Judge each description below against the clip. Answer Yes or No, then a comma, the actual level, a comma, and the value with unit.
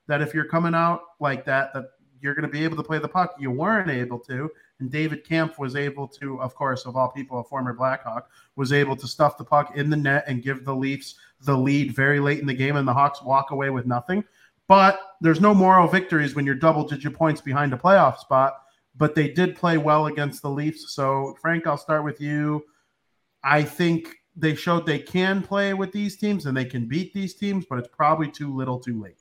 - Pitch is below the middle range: No, medium, 145 Hz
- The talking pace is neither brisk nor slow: No, fast, 230 wpm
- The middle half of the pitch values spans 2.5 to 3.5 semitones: Yes, average, 3.2 semitones